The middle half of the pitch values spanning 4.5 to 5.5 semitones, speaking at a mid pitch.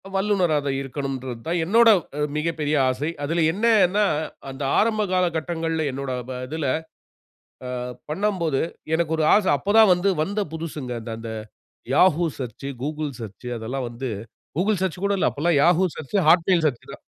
Yes: average, 5.2 semitones; medium, 160 Hz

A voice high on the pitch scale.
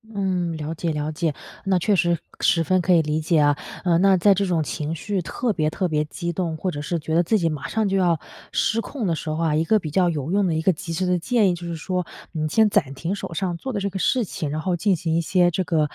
No: medium, 175 Hz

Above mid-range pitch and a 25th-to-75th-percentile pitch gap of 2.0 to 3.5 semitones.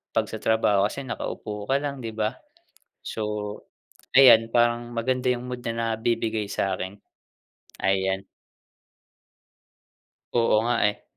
No: low, 115 Hz; narrow, 2.5 semitones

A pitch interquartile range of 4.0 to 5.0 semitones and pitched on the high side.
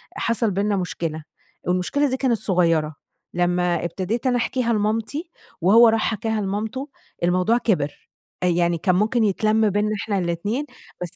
Yes: average, 4.3 semitones; high, 205 Hz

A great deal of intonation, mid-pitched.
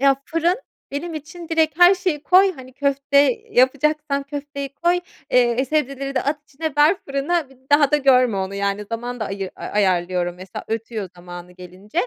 No: wide, 6.3 semitones; very high, 275 Hz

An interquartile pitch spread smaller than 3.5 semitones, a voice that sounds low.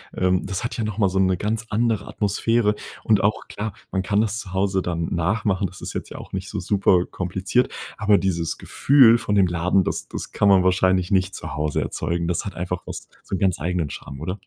Yes: narrow, 2.6 semitones; very low, 95 Hz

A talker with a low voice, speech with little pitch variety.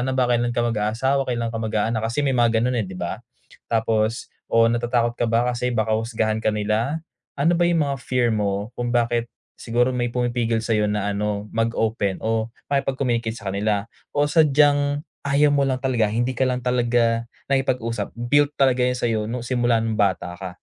Yes: low, 120 Hz; narrow, 2.3 semitones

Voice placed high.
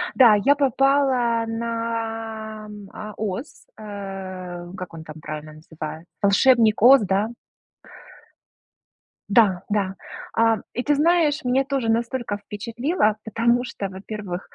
Yes: high, 220 Hz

